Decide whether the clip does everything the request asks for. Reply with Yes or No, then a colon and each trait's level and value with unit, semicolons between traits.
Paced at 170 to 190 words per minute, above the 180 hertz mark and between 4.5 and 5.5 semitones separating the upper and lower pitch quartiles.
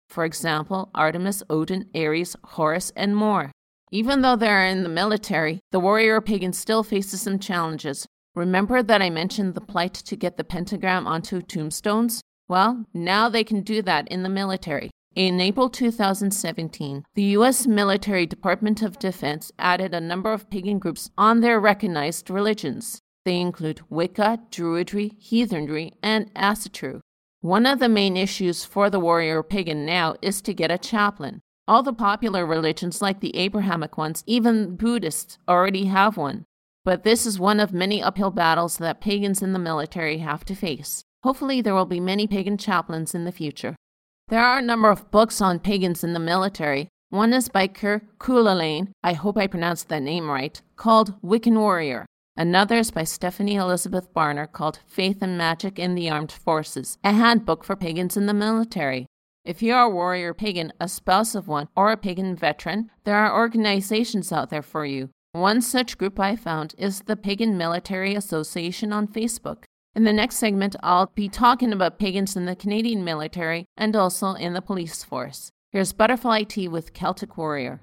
No: average, 175 wpm; high, 190 Hz; average, 3.8 semitones